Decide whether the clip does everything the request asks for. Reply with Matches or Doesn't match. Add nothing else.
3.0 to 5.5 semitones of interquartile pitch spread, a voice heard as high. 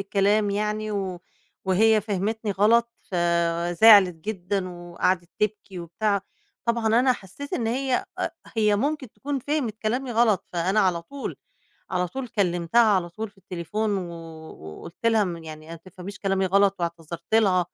Matches